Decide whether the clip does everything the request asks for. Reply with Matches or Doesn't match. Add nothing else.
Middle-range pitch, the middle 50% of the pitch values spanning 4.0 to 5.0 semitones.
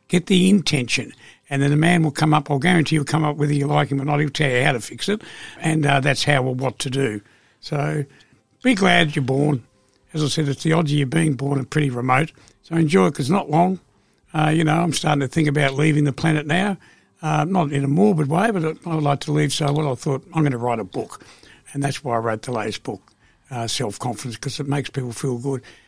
Doesn't match